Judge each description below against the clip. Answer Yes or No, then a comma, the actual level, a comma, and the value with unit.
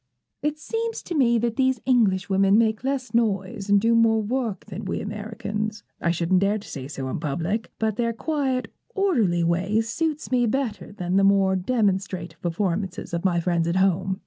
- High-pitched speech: Yes, high, 205 Hz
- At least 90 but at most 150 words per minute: No, average, 180 wpm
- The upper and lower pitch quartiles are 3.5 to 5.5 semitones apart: Yes, average, 4.1 semitones